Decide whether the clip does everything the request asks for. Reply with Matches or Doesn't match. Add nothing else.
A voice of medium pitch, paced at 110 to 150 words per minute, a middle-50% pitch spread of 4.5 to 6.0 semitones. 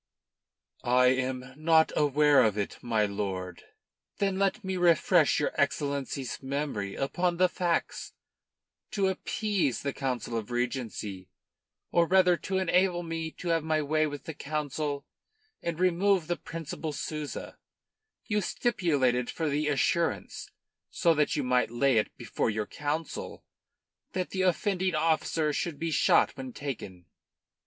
Matches